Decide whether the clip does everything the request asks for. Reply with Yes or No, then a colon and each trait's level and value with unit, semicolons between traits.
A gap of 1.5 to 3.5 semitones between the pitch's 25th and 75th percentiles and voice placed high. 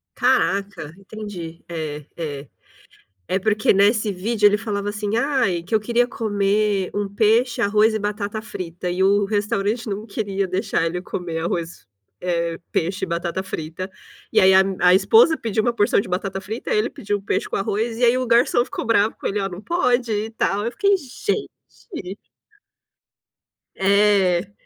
Yes: average, 3.0 semitones; high, 205 Hz